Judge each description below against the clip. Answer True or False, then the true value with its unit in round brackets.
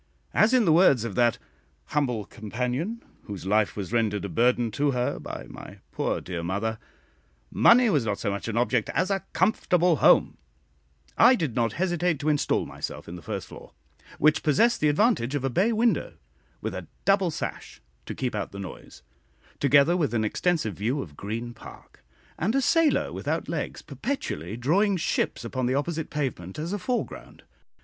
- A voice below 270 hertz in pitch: True (135 Hz)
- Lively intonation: True (8.2 semitones)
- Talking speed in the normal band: True (180 wpm)